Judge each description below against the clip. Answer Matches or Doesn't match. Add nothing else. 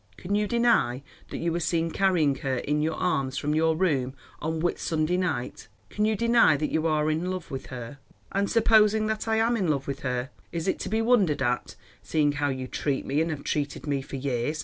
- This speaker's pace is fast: Matches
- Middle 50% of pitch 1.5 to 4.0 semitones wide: Doesn't match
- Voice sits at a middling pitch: Matches